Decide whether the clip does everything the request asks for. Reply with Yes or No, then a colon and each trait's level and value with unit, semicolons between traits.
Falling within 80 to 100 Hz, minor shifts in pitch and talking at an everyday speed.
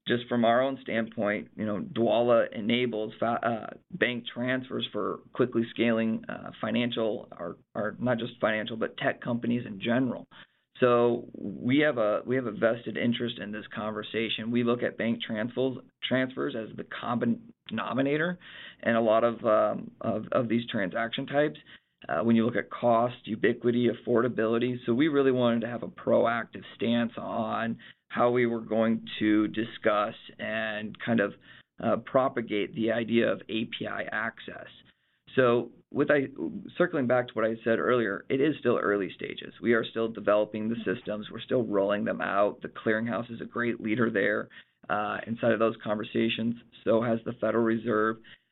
No: low, 115 Hz; narrow, 1.5 semitones; average, 170 wpm